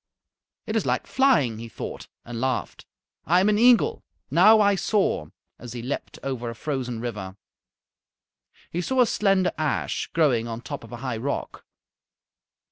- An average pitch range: No, wide, 8.9 semitones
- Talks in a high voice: No, low, 135 Hz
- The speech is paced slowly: No, average, 160 wpm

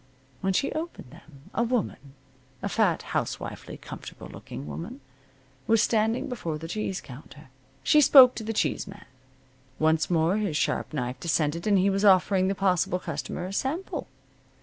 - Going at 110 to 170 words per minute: Yes, average, 160 wpm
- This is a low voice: No, high, 190 Hz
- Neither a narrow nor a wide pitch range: No, wide, 5.8 semitones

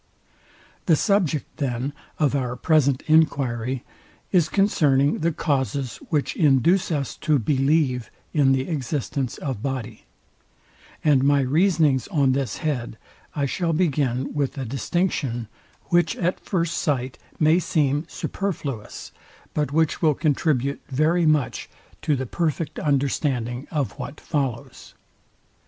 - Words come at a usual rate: No, slow, 125 wpm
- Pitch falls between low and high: Yes, medium, 145 Hz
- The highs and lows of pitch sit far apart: No, average, 3.2 semitones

